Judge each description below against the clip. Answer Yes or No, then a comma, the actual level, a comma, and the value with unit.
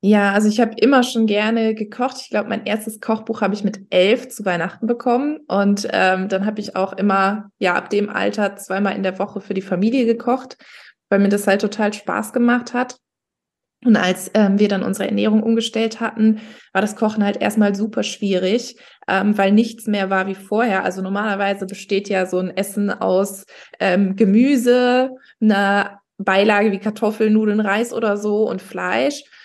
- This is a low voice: No, high, 210 Hz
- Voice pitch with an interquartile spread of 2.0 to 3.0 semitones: Yes, narrow, 2.6 semitones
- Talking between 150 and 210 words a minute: Yes, average, 180 wpm